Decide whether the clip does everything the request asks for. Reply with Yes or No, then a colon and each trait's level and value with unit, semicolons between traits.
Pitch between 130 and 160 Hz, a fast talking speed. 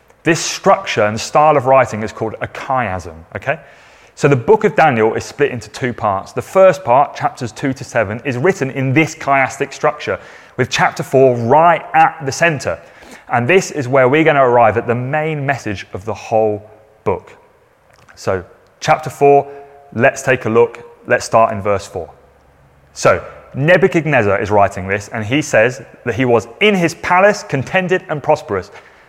No: low, 135 Hz; average, 175 wpm